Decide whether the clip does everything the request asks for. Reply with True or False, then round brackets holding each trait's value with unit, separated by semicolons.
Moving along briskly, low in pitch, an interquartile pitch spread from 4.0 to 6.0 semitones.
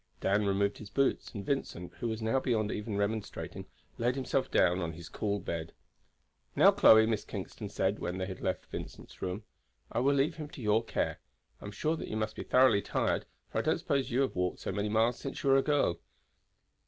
True (215 wpm; 110 Hz; 4.5 semitones)